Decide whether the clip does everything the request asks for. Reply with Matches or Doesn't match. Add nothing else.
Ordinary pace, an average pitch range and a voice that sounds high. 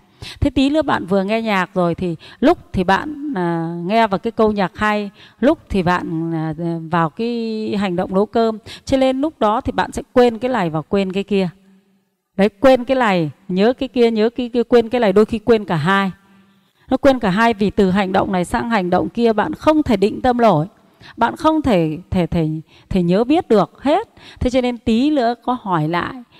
Matches